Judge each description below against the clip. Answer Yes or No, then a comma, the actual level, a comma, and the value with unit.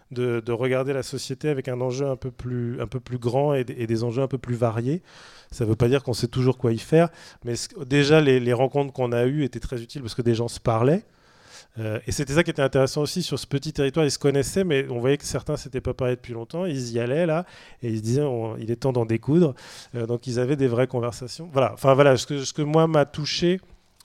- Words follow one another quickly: Yes, fast, 270 wpm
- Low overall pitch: Yes, low, 130 Hz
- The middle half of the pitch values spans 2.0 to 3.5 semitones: Yes, average, 3.1 semitones